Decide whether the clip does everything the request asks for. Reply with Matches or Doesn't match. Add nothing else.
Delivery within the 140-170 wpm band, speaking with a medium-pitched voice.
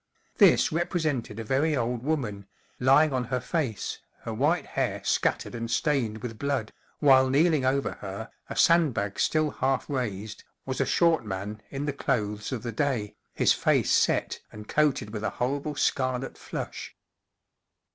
Doesn't match